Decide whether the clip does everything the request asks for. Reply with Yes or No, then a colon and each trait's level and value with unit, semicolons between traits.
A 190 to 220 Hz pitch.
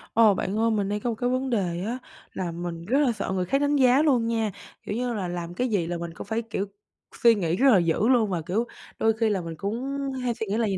Yes: high, 215 Hz